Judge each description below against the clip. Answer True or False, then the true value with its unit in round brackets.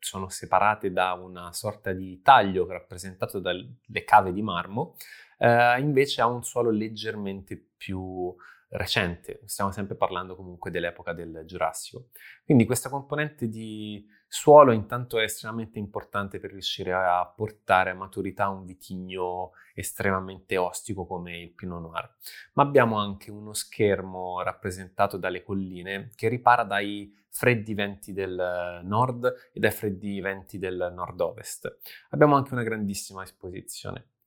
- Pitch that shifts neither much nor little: True (3.4 semitones)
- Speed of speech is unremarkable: True (135 wpm)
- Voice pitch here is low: True (100 Hz)